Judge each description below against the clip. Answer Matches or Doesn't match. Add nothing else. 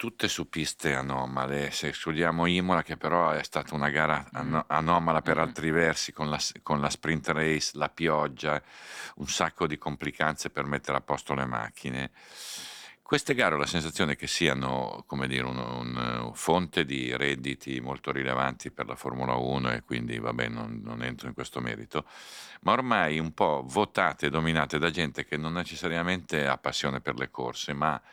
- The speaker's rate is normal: Doesn't match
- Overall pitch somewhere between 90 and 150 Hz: Doesn't match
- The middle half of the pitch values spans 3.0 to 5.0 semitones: Matches